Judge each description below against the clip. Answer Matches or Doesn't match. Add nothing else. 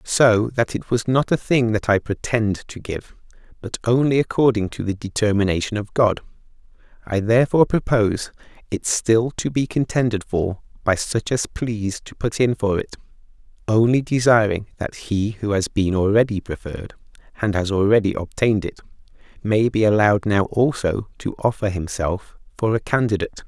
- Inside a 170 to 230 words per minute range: Doesn't match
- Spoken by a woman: Doesn't match